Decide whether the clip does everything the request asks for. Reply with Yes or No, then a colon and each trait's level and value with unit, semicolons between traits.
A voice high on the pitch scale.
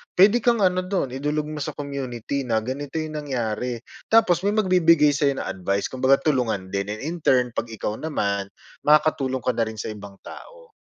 No: low, 135 Hz